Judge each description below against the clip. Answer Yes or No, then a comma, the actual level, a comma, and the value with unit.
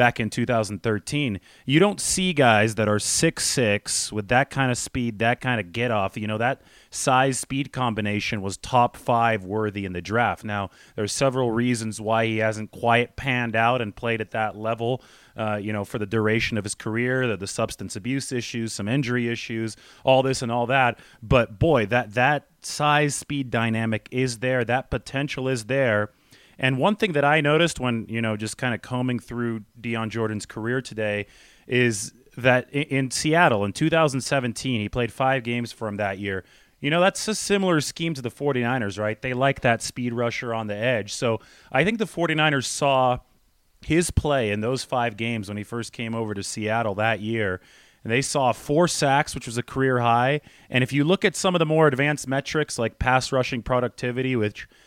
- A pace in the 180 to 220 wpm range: Yes, average, 190 wpm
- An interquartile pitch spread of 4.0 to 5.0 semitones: No, average, 3.5 semitones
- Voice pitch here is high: No, low, 120 Hz